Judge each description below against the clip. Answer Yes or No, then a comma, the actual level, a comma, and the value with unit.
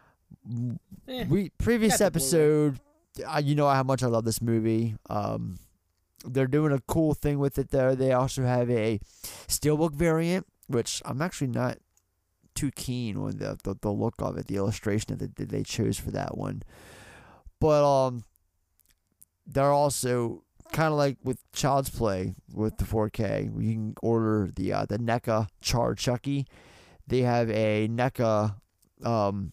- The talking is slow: No, average, 155 wpm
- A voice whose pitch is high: No, low, 120 Hz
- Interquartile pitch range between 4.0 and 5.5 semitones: Yes, average, 5.1 semitones